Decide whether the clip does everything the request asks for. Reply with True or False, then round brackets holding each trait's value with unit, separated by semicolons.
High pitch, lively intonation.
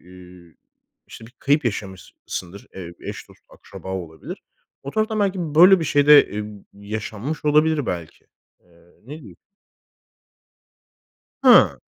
False (115 Hz; 8.5 semitones)